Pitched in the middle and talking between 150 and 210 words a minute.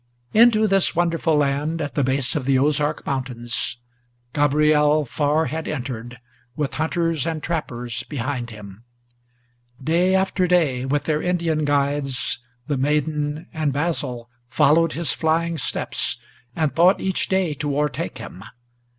No: medium, 150 Hz; slow, 135 wpm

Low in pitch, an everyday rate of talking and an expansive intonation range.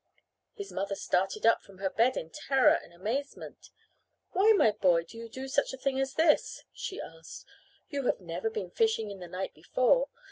No: high, 230 Hz; average, 190 wpm; wide, 7.0 semitones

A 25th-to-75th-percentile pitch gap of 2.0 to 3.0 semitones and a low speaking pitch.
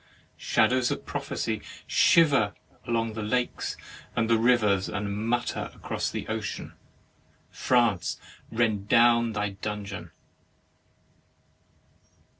Yes: narrow, 2.6 semitones; low, 110 Hz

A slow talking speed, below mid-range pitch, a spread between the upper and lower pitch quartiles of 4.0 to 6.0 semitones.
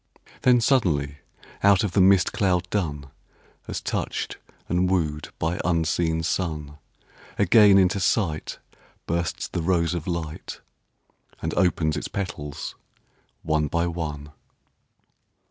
No: slow, 115 wpm; very low, 85 Hz; average, 3.4 semitones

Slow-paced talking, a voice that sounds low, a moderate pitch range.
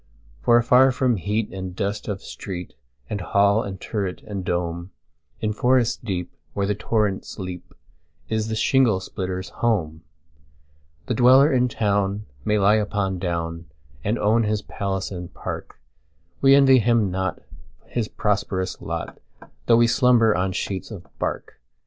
Yes: slow, 130 wpm; low, 100 Hz; average, 4.0 semitones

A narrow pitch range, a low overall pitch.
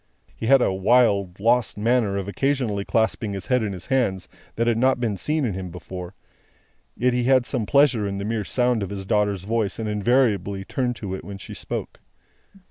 No: average, 3.9 semitones; low, 110 Hz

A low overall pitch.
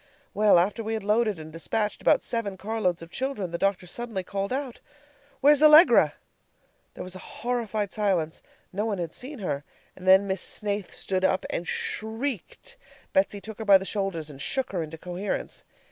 No: high, 200 Hz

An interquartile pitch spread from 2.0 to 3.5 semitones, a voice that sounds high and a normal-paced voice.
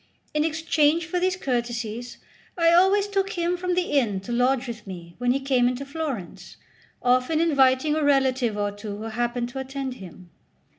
No: average, 5.1 semitones; very high, 260 Hz; average, 180 wpm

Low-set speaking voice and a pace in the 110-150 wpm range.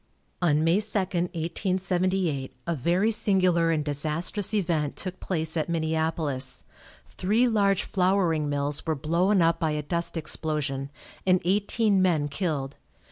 No: medium, 170 Hz; slow, 135 wpm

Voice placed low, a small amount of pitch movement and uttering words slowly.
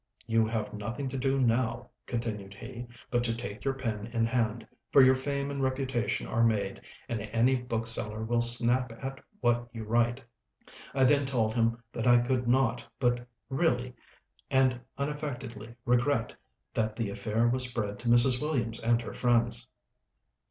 No: low, 120 Hz; narrow, 2.2 semitones; average, 160 wpm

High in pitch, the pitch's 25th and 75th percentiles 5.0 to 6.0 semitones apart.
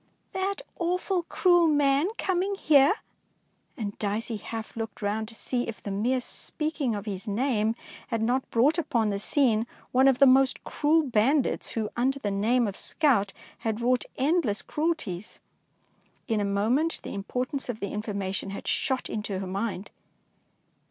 Yes: high, 240 Hz; wide, 5.5 semitones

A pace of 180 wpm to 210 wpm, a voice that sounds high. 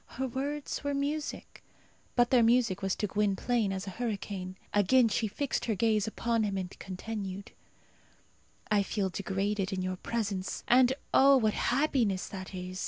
No: average, 160 wpm; high, 210 Hz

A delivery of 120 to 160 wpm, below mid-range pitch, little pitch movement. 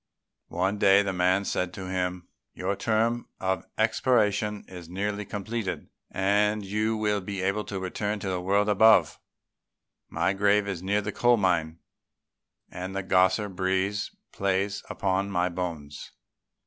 Yes: average, 150 wpm; low, 100 Hz; narrow, 2.0 semitones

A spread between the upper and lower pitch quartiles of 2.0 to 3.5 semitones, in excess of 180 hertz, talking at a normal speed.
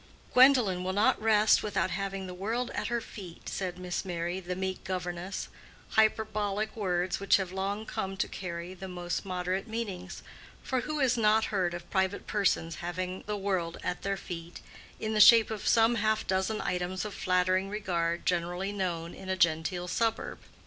Yes: average, 2.9 semitones; high, 190 Hz; average, 175 wpm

